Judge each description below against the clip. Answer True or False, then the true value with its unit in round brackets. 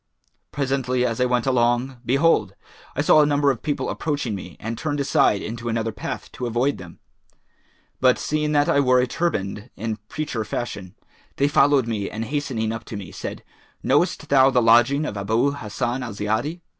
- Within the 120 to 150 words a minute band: False (180 wpm)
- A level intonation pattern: False (4.0 semitones)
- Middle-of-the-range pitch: False (125 Hz)